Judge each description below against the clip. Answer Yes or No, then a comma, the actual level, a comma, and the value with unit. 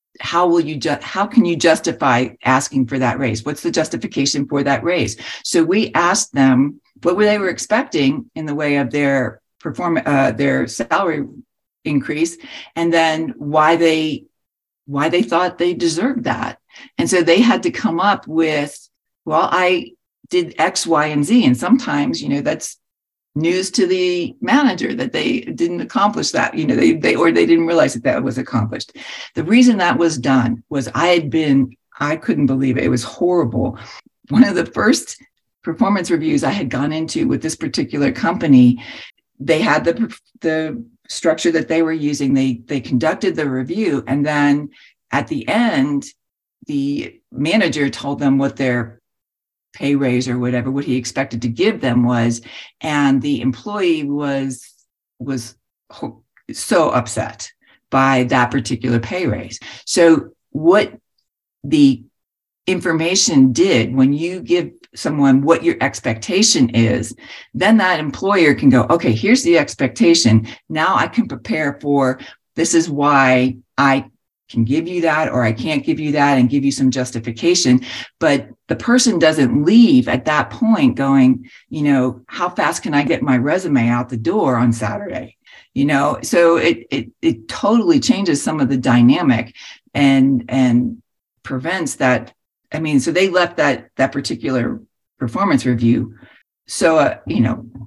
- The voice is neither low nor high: Yes, medium, 145 Hz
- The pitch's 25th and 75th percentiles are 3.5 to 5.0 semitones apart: No, wide, 5.6 semitones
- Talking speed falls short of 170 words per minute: Yes, average, 160 wpm